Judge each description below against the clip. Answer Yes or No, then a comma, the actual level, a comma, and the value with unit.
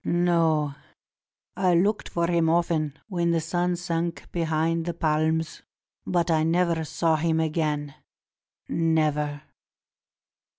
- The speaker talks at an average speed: No, slow, 120 wpm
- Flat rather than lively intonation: Yes, narrow, 1.6 semitones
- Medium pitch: Yes, medium, 165 Hz